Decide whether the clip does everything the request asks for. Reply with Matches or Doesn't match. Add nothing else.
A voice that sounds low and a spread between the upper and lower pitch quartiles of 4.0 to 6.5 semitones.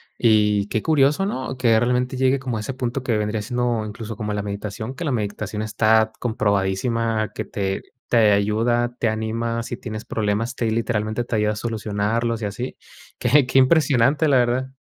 Doesn't match